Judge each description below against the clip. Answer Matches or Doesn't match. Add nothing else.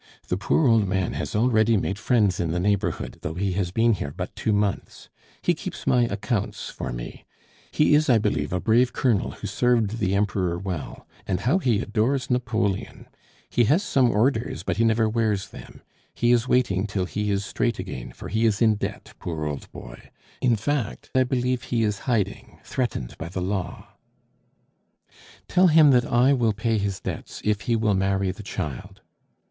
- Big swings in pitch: Doesn't match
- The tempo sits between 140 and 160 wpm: Doesn't match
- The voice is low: Matches